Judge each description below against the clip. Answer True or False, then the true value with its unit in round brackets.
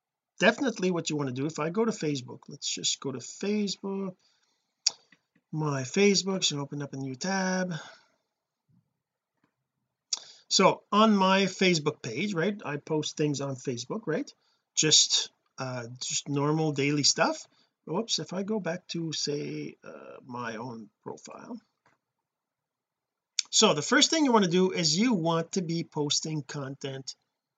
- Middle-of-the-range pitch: True (160 Hz)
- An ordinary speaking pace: True (150 wpm)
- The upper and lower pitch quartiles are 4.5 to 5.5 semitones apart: True (5.2 semitones)